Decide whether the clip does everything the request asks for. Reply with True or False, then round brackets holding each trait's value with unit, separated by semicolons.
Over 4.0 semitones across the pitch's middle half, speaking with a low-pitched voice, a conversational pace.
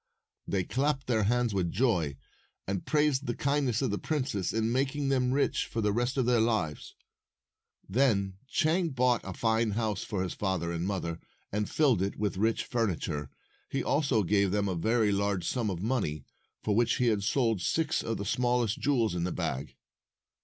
True (4.6 semitones; 110 Hz; 185 wpm)